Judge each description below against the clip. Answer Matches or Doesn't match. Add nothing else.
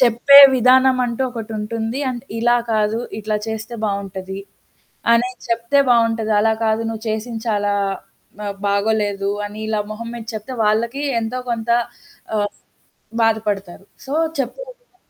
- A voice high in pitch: Matches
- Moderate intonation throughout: Doesn't match